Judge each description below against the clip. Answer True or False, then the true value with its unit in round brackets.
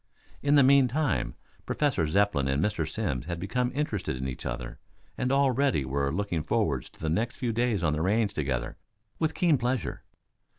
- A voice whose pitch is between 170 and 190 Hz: False (100 Hz)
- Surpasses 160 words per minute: True (175 wpm)